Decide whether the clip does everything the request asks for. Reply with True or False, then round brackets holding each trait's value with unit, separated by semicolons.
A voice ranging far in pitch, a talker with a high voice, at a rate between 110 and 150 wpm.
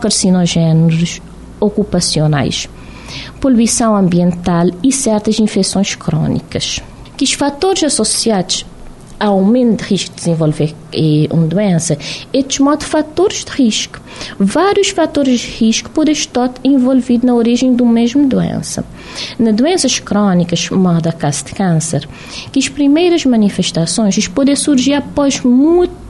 True (7.4 semitones; 220 Hz; 120 wpm)